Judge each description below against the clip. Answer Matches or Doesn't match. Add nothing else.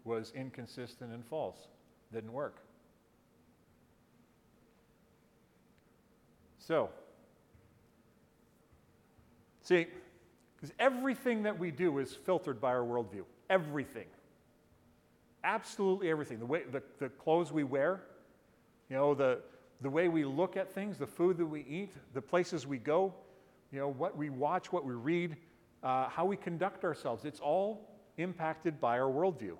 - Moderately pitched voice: Matches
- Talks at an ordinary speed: Doesn't match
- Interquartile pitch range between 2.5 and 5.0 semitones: Doesn't match